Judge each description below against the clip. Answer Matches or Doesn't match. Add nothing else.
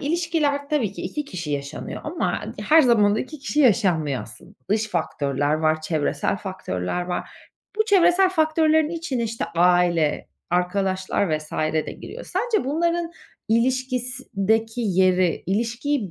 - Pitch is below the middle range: Doesn't match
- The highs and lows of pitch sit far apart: Matches